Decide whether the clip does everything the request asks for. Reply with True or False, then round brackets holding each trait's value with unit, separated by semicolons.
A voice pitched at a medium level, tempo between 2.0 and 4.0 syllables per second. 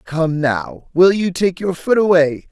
True (170 Hz; 3.8 syllables/s)